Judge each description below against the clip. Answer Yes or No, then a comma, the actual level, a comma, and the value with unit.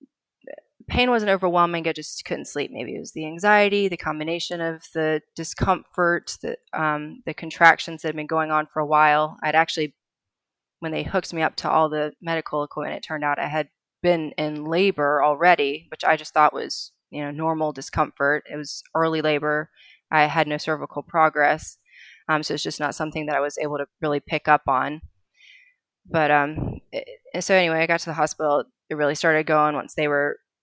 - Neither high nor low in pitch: Yes, medium, 155 Hz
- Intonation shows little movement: Yes, narrow, 1.8 semitones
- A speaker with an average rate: Yes, average, 195 wpm